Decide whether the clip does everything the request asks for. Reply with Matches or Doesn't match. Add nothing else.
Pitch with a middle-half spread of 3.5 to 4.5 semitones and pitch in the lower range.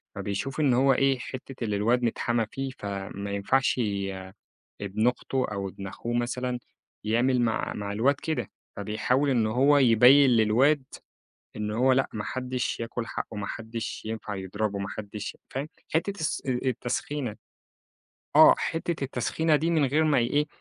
Matches